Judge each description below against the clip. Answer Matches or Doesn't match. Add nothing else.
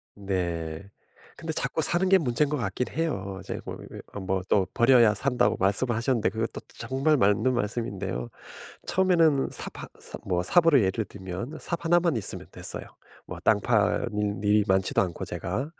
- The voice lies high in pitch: Doesn't match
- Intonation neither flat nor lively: Doesn't match